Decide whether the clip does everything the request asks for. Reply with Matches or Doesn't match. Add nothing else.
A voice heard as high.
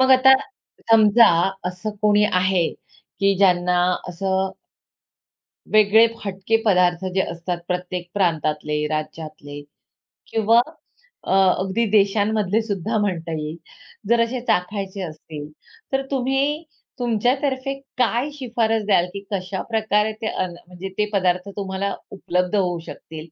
Matches